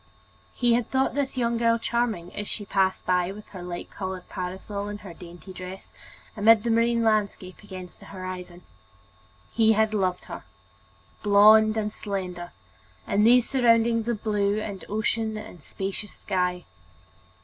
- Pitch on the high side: Yes, high, 205 Hz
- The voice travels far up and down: No, average, 3.5 semitones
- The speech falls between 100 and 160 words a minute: Yes, average, 150 wpm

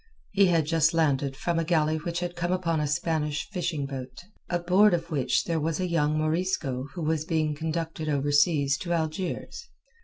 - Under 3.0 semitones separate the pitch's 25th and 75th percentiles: Yes, narrow, 2.4 semitones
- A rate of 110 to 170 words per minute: No, average, 185 wpm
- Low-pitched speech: No, medium, 160 Hz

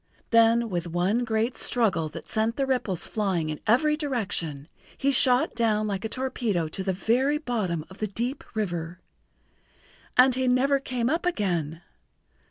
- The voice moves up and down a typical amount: No, wide, 5.7 semitones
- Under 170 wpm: Yes, average, 160 wpm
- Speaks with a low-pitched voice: No, high, 220 Hz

